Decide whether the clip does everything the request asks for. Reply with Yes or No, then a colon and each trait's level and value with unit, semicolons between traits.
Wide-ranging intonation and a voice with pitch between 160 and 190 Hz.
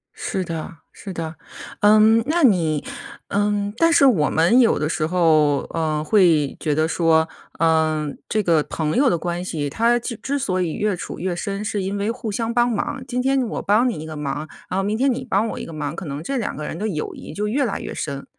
Yes: wide, 6.0 semitones; medium, 185 Hz